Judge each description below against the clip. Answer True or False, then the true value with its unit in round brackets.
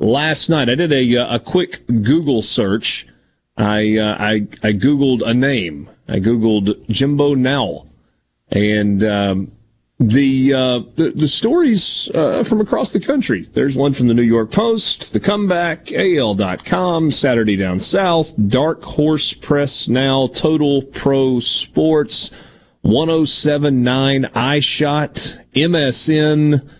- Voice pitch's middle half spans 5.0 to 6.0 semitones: True (5.4 semitones)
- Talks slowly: True (130 wpm)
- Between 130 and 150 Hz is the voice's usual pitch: True (135 Hz)